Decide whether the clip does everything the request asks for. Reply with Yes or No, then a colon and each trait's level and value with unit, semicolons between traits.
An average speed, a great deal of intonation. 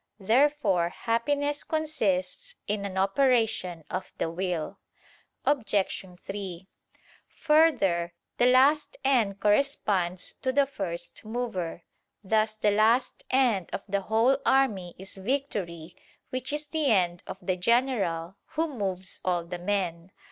No: slow, 125 wpm; wide, 6.3 semitones